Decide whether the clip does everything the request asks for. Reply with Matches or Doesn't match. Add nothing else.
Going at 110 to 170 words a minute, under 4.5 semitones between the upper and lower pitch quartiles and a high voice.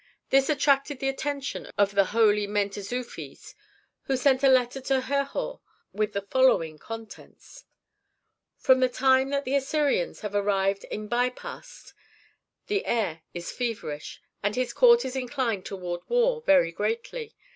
Doesn't match